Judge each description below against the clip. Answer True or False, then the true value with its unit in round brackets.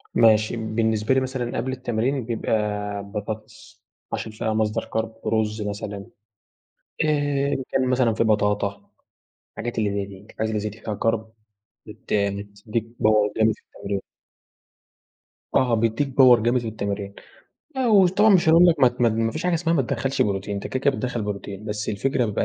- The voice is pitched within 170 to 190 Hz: False (110 Hz)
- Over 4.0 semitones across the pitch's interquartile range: False (3.4 semitones)